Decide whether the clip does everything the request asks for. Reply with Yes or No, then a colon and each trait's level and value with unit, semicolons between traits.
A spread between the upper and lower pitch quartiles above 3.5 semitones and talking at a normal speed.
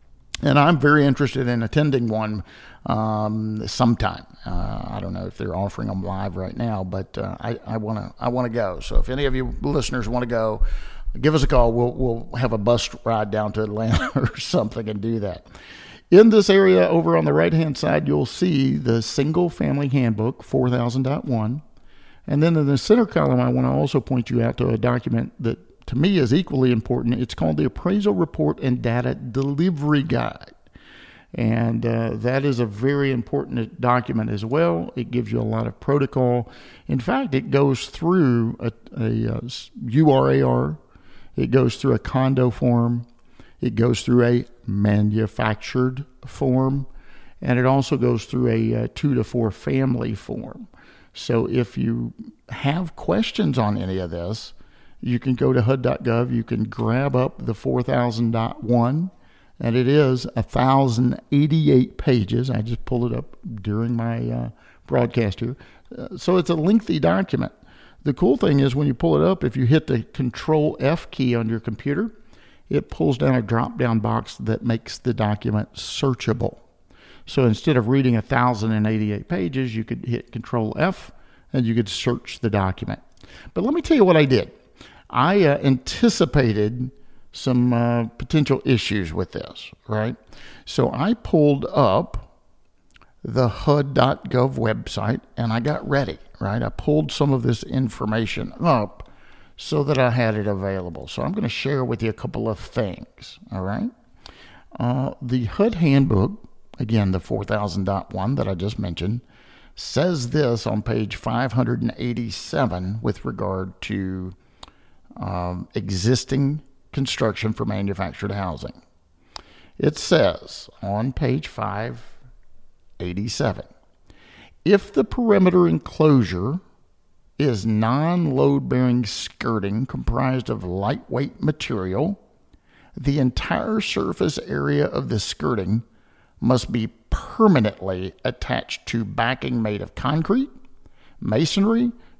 Yes: average, 3.9 semitones; average, 150 wpm